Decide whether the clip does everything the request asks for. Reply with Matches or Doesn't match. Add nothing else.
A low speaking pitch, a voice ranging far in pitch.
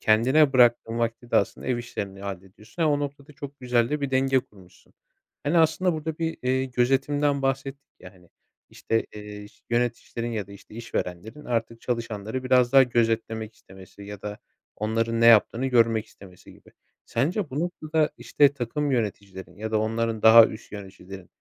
Doesn't match